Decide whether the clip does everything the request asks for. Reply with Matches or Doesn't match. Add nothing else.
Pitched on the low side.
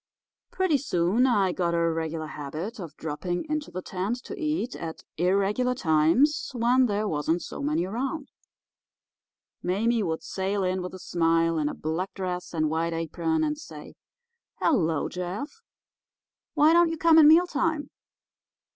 Doesn't match